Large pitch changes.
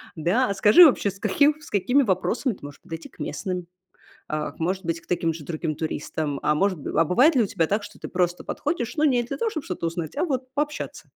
Yes: wide, 7.6 semitones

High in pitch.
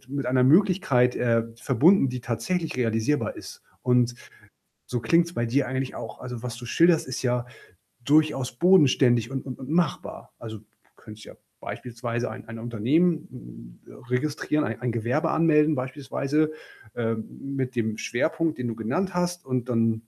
No: low, 125 Hz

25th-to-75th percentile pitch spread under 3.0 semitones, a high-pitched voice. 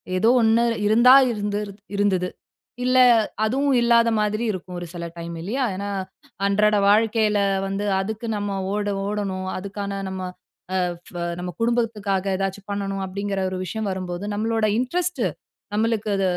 Yes: narrow, 2.4 semitones; high, 205 Hz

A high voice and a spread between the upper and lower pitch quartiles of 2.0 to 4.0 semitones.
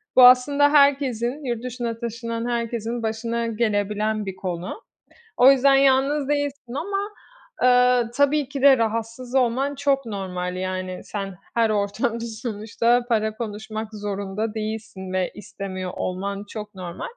Yes: high, 230 Hz; average, 3.7 semitones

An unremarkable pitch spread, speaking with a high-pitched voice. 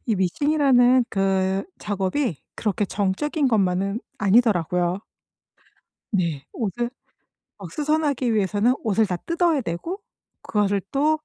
No: wide, 6.0 semitones; high, 210 Hz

